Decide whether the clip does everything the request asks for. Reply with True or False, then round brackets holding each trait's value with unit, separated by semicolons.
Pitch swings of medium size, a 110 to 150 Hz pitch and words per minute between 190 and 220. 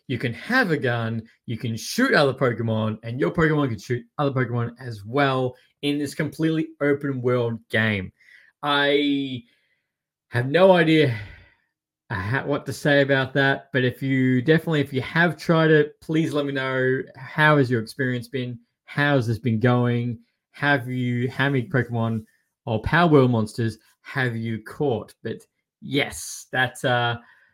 False (3.4 semitones; 130 Hz; 160 wpm)